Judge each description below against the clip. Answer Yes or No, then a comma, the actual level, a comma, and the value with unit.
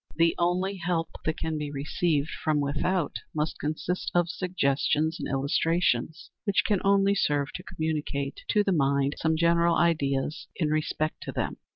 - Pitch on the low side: No, medium, 160 Hz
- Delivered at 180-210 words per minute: No, average, 160 wpm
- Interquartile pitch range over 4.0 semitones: No, average, 3.2 semitones